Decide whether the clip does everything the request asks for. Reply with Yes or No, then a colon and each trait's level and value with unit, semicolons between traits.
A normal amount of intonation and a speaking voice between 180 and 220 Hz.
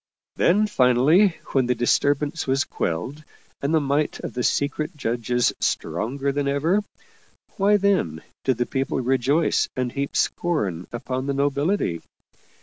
No: average, 3.7 semitones; medium, 140 Hz